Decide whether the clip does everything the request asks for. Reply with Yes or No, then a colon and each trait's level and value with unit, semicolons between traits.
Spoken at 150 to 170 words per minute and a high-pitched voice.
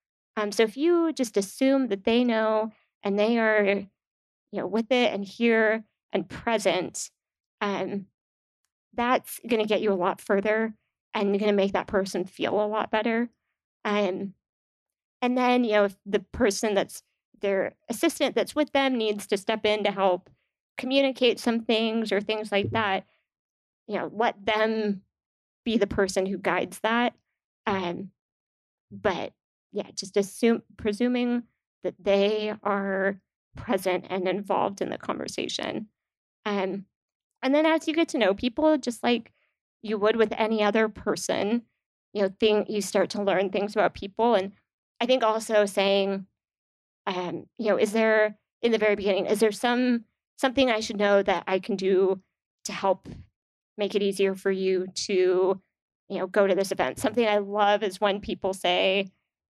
Yes: average, 165 wpm; high, 210 Hz